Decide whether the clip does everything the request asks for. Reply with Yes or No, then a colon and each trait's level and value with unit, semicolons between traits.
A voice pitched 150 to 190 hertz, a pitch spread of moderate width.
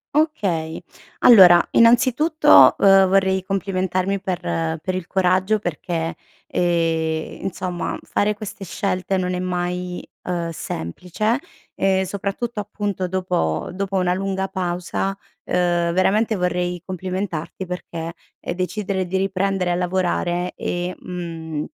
No: medium, 185 Hz; narrow, 1.8 semitones